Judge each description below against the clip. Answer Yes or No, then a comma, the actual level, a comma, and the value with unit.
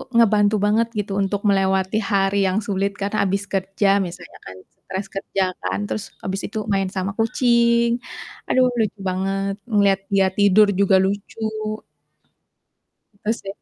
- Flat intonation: Yes, narrow, 1.5 semitones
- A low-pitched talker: No, high, 200 Hz